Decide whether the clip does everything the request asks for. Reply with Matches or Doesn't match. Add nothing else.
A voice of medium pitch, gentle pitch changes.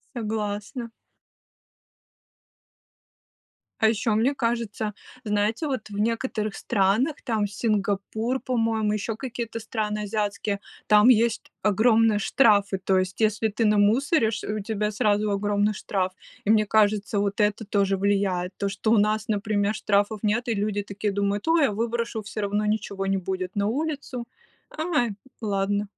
Doesn't match